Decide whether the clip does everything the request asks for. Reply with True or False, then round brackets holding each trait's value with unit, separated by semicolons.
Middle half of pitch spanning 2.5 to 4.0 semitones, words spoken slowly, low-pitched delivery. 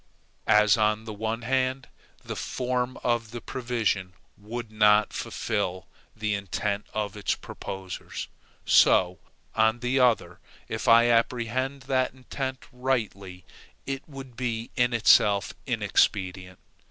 True (3.3 semitones; 120 wpm; 115 Hz)